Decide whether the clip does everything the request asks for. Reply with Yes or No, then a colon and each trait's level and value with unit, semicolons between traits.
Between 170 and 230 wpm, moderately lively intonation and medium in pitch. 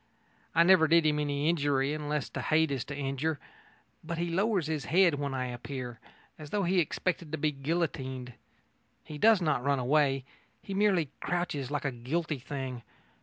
Yes: average, 175 wpm; average, 3.7 semitones; medium, 150 Hz